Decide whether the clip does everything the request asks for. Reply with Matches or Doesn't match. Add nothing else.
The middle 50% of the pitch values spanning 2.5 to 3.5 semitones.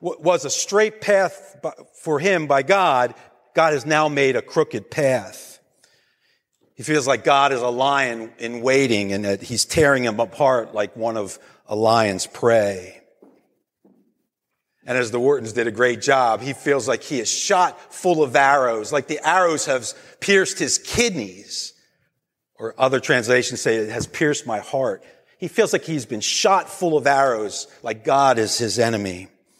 Doesn't match